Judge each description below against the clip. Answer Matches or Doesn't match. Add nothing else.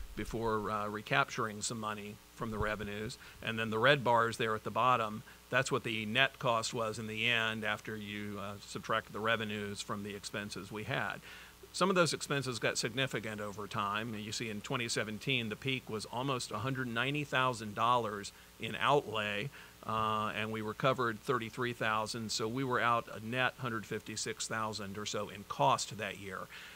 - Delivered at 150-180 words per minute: Matches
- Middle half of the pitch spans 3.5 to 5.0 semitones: Doesn't match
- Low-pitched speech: Matches